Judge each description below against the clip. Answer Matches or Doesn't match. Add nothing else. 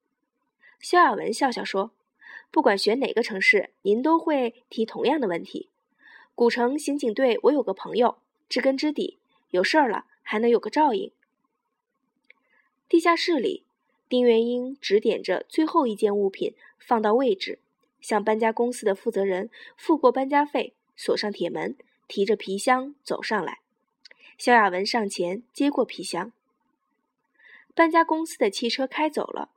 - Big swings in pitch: Matches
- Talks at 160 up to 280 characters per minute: Matches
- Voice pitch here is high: Matches